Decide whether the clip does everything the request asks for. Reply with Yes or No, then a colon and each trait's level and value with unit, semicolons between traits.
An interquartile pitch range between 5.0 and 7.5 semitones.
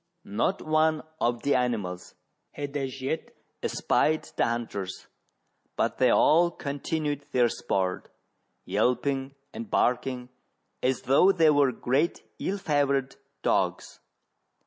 No: average, 3.8 semitones